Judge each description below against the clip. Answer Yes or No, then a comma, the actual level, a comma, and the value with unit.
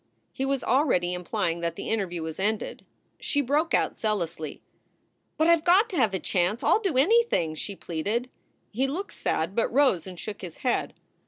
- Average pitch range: No, wide, 8.5 semitones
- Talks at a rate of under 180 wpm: No, average, 190 wpm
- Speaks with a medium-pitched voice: No, high, 220 Hz